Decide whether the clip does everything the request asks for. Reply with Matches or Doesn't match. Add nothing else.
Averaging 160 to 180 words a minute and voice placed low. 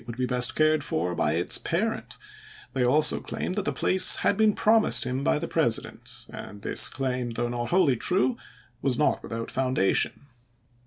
Matches